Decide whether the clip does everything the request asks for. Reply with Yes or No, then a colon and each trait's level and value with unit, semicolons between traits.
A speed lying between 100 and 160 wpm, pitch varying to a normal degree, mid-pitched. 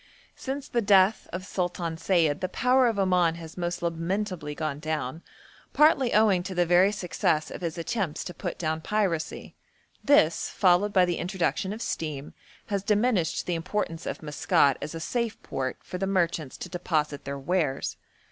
No: average, 170 wpm; average, 3.8 semitones; medium, 175 Hz